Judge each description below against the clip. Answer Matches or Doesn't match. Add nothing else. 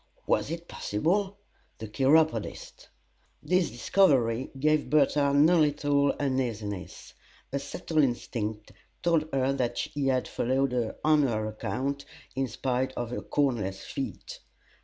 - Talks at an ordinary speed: Doesn't match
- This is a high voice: Doesn't match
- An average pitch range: Matches